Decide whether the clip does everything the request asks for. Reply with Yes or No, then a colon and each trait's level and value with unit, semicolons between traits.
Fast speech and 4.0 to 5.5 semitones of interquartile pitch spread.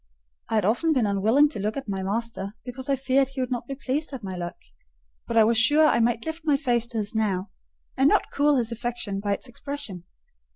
Yes: fast, 235 wpm; average, 4.5 semitones